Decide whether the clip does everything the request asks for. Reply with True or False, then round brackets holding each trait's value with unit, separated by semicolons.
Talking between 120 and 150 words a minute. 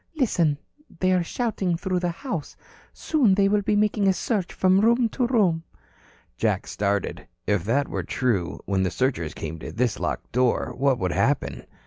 False (175 wpm)